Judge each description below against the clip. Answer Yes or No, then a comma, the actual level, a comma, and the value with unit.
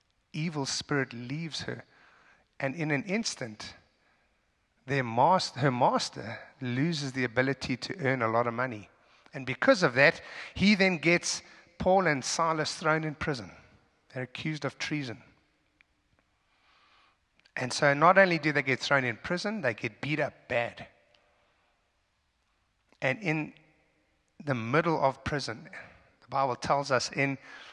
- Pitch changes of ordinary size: Yes, average, 4.1 semitones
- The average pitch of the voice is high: No, medium, 140 Hz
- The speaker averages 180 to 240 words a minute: No, average, 140 wpm